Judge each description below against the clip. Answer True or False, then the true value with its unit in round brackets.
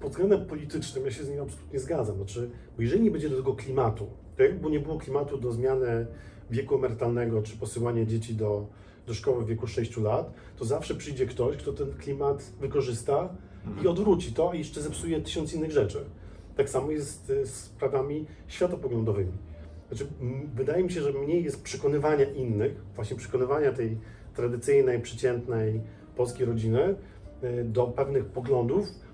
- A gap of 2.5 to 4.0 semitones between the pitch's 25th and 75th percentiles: False (4.4 semitones)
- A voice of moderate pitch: False (125 Hz)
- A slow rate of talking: False (165 wpm)